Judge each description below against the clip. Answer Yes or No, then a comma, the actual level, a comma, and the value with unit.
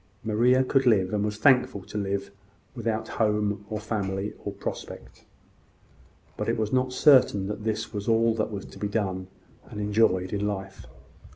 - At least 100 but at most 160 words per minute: No, average, 170 wpm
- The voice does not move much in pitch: Yes, narrow, 2.1 semitones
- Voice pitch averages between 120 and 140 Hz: No, low, 105 Hz